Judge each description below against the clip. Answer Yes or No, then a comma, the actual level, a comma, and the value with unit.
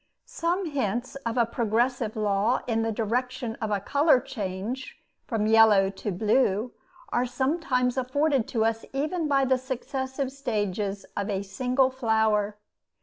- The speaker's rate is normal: Yes, average, 145 wpm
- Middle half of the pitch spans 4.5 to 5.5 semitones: No, average, 3.7 semitones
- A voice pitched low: No, high, 240 Hz